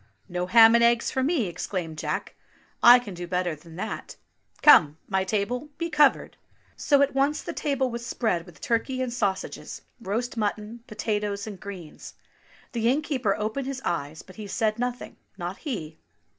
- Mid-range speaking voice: No, high, 220 Hz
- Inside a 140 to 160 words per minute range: No, average, 175 wpm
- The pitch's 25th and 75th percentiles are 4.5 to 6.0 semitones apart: Yes, average, 4.9 semitones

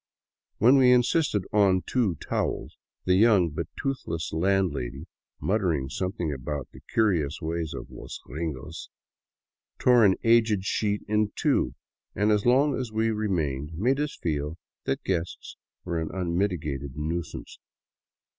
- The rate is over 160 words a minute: No, slow, 135 wpm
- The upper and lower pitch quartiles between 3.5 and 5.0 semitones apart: No, wide, 5.5 semitones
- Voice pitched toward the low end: Yes, very low, 95 Hz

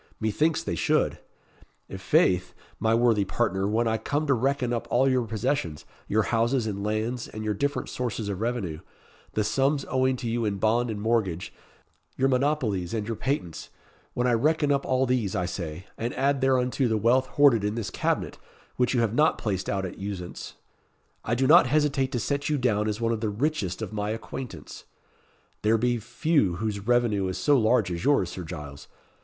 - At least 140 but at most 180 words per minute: No, average, 195 wpm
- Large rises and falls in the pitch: No, average, 4.1 semitones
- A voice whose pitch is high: No, low, 115 Hz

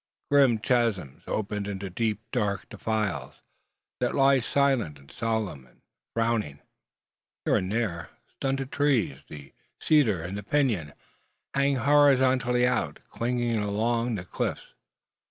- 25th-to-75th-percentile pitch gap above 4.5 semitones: Yes, average, 5.0 semitones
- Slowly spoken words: Yes, slow, 120 wpm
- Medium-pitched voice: No, low, 115 Hz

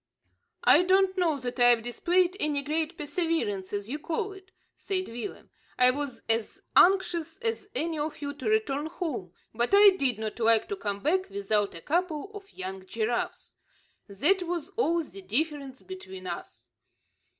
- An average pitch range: No, wide, 8.2 semitones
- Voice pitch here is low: No, very high, 295 Hz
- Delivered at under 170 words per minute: Yes, average, 160 wpm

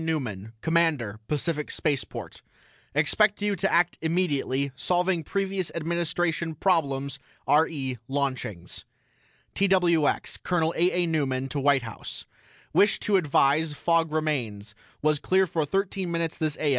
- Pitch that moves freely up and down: No, average, 3.9 semitones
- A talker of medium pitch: Yes, medium, 160 Hz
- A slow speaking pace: Yes, slow, 125 wpm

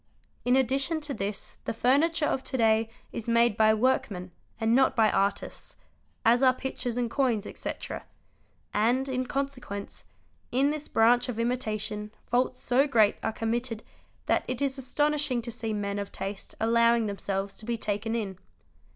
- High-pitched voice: Yes, high, 235 Hz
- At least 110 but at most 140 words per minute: No, average, 165 wpm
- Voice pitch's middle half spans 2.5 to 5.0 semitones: Yes, average, 3.3 semitones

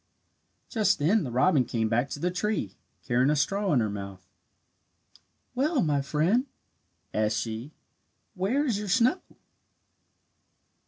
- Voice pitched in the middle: Yes, medium, 150 Hz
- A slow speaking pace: Yes, slow, 130 wpm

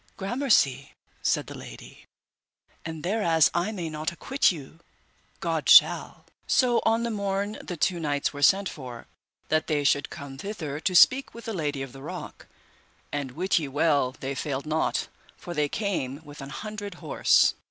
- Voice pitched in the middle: Yes, medium, 160 Hz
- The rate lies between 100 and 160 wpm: No, average, 170 wpm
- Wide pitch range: Yes, wide, 5.8 semitones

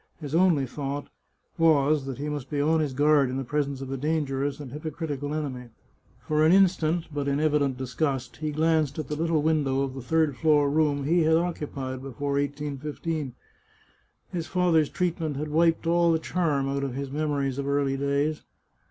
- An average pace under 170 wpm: No, average, 185 wpm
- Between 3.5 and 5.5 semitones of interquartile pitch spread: No, narrow, 2.4 semitones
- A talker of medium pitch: Yes, medium, 145 Hz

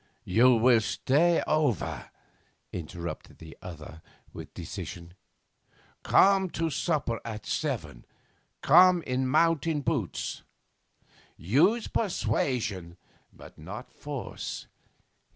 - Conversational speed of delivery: No, slow, 90 wpm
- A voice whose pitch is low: Yes, low, 125 Hz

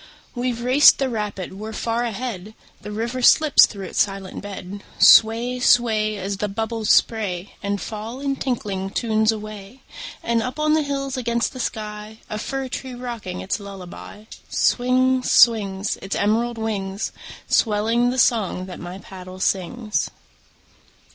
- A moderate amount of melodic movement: Yes, average, 3.5 semitones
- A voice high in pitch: Yes, high, 220 Hz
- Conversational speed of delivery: Yes, average, 150 wpm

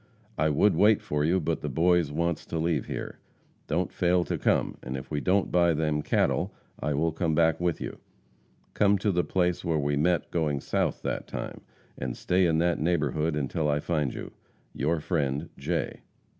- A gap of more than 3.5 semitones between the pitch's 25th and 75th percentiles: No, average, 2.9 semitones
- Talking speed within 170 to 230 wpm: Yes, average, 190 wpm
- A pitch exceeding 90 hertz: No, very low, 80 Hz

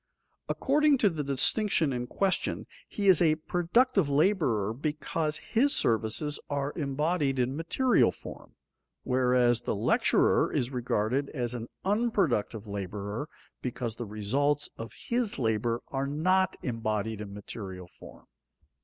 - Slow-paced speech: Yes, slow, 125 wpm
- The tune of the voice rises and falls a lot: Yes, wide, 6.7 semitones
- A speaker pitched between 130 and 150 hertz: Yes, low, 135 Hz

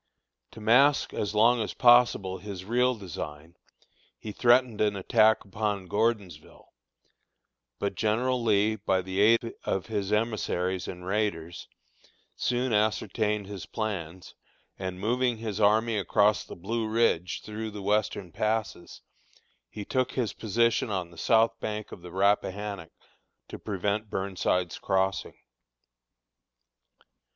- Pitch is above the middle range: No, low, 105 Hz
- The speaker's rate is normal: No, slow, 125 wpm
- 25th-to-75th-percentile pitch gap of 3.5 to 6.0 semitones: No, average, 2.9 semitones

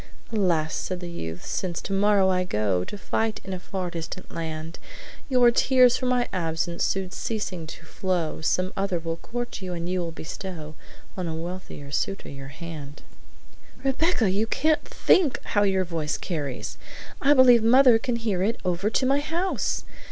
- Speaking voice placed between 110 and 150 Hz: No, medium, 185 Hz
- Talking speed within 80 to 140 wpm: No, average, 170 wpm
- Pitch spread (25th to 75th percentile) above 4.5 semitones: Yes, wide, 5.4 semitones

